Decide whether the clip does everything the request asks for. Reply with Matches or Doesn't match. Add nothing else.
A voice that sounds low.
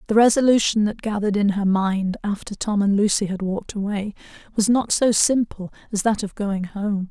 Doesn't match